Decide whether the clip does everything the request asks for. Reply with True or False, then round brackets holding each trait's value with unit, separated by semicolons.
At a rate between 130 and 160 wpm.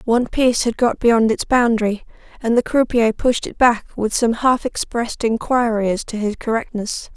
False (185 wpm)